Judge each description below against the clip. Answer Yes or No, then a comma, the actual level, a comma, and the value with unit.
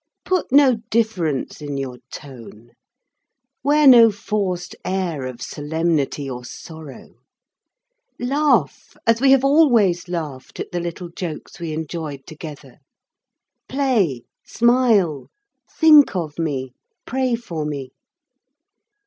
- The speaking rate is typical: No, slow, 110 wpm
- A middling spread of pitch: No, wide, 8.5 semitones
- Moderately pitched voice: Yes, medium, 170 Hz